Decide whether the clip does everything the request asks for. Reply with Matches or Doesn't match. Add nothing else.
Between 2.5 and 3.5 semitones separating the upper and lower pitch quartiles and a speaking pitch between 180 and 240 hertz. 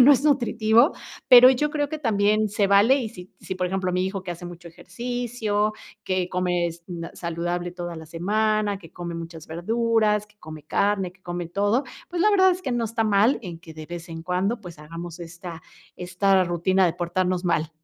Doesn't match